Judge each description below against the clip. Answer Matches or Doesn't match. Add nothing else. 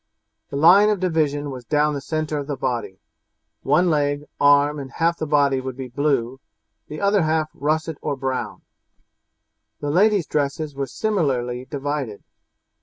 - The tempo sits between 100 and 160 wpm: Matches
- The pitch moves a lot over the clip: Doesn't match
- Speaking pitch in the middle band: Matches